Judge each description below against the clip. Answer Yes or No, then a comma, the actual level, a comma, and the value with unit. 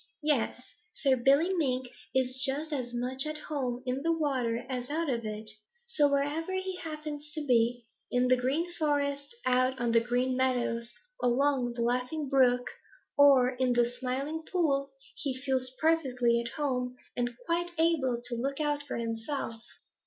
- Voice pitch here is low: No, very high, 260 Hz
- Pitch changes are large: No, average, 3.2 semitones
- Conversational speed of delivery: Yes, average, 160 wpm